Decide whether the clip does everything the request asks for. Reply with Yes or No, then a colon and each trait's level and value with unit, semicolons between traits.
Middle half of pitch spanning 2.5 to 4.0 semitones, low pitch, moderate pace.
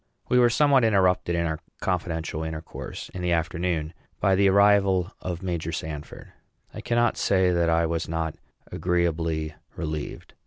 Yes: average, 2.9 semitones; very low, 85 Hz; average, 150 wpm